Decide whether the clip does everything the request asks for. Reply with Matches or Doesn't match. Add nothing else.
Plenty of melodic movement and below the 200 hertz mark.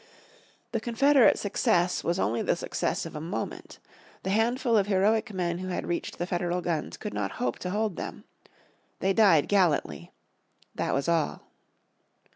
Doesn't match